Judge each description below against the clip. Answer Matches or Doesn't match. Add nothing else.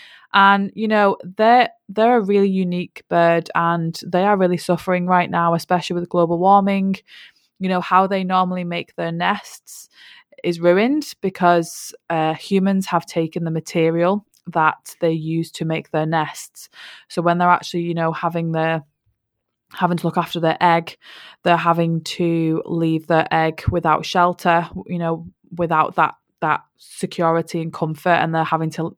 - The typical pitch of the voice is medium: Matches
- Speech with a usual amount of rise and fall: Doesn't match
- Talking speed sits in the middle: Matches